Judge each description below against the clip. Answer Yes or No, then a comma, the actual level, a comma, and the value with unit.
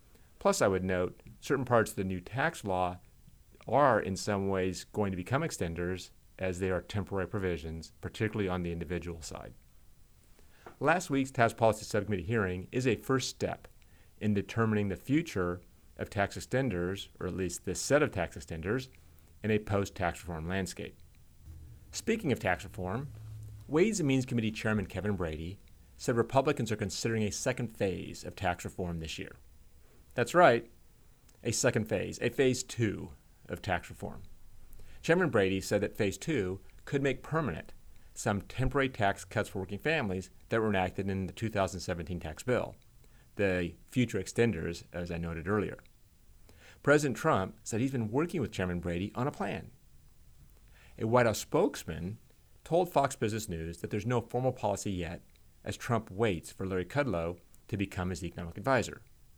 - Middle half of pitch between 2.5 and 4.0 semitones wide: No, average, 4.5 semitones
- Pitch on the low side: Yes, low, 100 Hz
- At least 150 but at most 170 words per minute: Yes, average, 165 wpm